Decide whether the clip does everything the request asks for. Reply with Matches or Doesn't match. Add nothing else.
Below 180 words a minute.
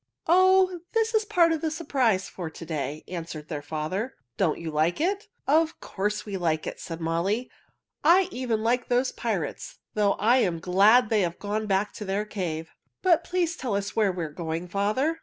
Doesn't match